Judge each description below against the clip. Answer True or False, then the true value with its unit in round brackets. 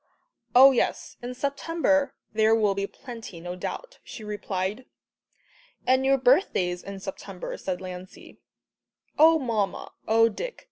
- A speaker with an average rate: False (130 wpm)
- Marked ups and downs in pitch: True (5.7 semitones)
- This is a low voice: False (225 Hz)